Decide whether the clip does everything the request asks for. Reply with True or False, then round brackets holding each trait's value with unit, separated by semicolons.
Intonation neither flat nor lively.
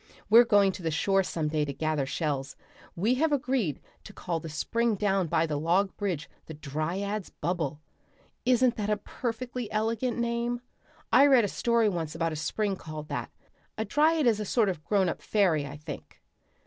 False (6.5 semitones)